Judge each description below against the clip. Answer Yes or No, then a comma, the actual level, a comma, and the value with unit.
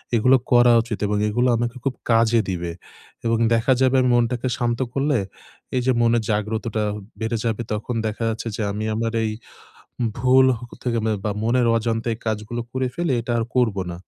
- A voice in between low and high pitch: No, low, 115 Hz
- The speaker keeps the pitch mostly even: Yes, narrow, 1.9 semitones